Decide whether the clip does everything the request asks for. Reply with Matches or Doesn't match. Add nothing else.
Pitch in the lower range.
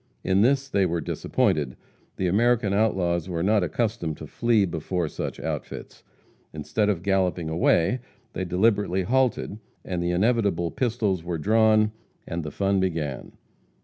Matches